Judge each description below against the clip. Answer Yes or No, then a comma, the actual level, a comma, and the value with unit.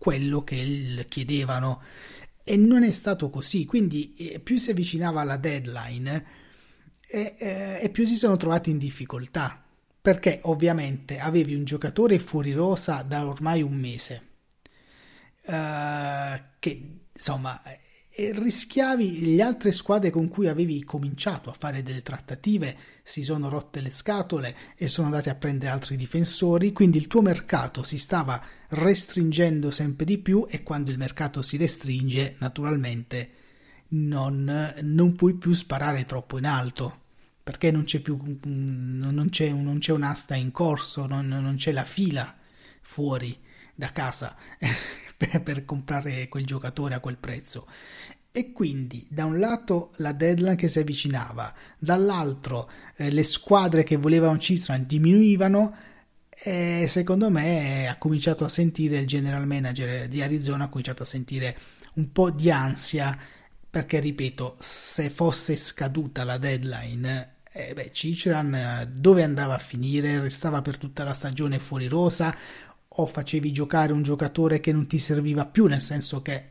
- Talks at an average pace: Yes, average, 145 wpm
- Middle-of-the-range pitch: Yes, medium, 150 Hz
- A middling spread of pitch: Yes, average, 3.8 semitones